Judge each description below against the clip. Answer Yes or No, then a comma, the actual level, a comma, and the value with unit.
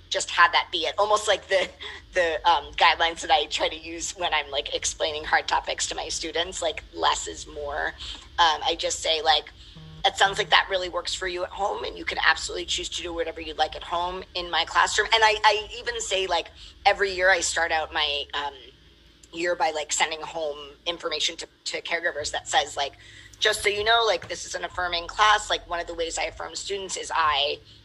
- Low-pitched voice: No, medium, 175 Hz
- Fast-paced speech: Yes, fast, 225 wpm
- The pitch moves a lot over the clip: No, average, 4.3 semitones